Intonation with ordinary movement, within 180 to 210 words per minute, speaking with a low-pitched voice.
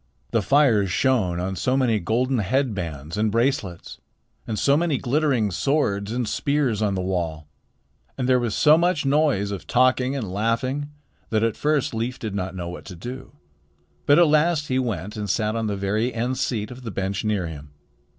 Yes: average, 5.0 semitones; average, 190 wpm; low, 115 Hz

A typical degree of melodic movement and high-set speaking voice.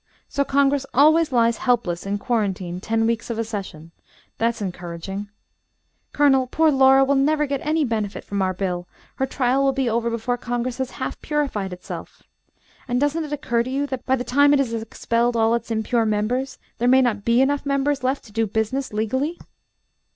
Yes: average, 3.8 semitones; high, 245 Hz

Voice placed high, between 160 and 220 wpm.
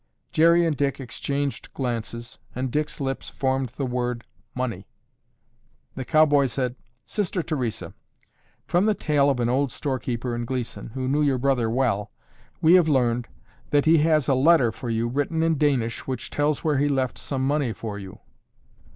No: low, 135 Hz; average, 170 wpm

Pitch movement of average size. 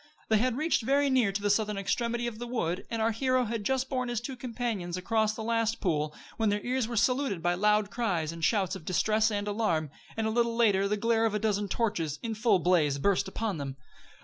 Yes: average, 3.4 semitones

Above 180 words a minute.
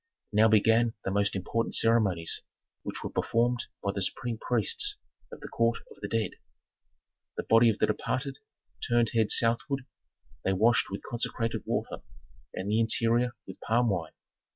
No: average, 155 wpm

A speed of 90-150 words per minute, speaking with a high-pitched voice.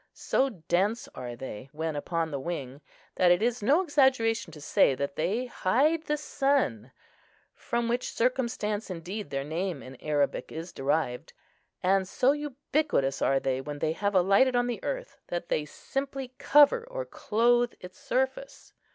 No: average, 160 wpm; high, 200 Hz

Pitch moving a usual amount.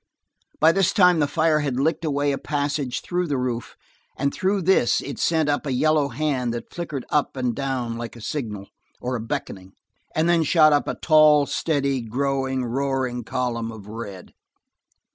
Yes: average, 3.9 semitones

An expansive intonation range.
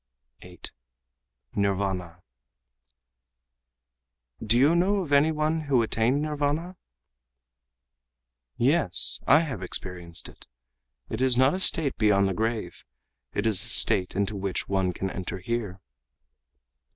Yes: wide, 7.0 semitones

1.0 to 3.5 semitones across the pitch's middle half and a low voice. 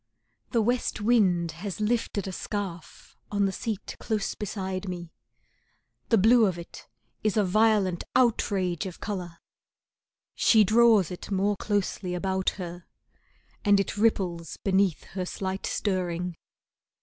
No: average, 2.9 semitones; high, 195 Hz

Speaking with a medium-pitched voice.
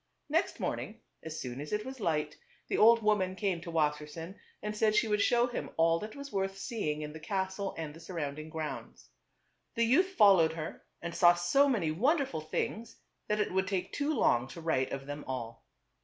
Yes: medium, 180 Hz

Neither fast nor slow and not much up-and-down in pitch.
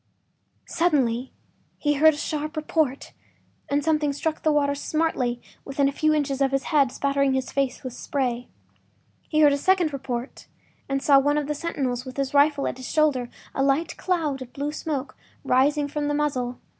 Yes: average, 180 wpm; narrow, 2.2 semitones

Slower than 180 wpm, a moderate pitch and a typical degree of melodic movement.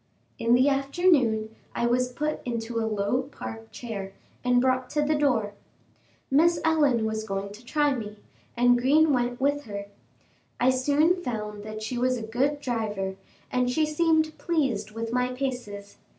No: average, 165 wpm; high, 245 Hz; average, 4.6 semitones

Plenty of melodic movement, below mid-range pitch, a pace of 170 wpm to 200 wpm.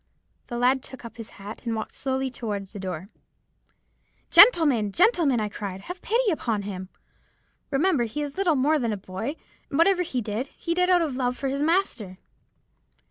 No: wide, 7.4 semitones; very high, 260 Hz; average, 180 wpm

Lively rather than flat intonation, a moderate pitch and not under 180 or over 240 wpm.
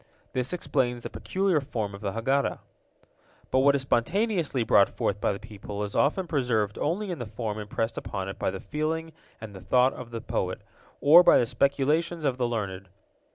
No: wide, 6.2 semitones; low, 125 Hz; average, 195 wpm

